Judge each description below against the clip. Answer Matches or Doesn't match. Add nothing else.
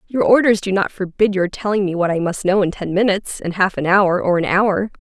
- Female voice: Matches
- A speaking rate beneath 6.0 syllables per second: Matches